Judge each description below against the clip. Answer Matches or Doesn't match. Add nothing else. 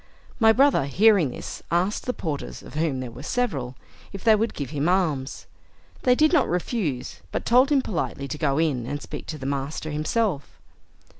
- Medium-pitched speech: Matches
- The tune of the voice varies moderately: Doesn't match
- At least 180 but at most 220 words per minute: Matches